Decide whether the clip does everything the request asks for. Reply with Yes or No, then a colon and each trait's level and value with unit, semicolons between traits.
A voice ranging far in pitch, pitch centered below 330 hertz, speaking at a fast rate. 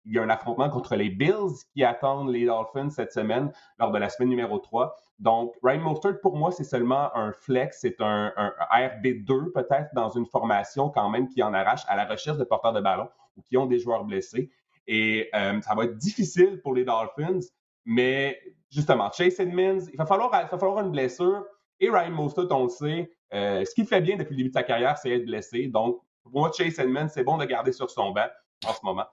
Yes: wide, 7.1 semitones; low, 135 Hz; fast, 230 wpm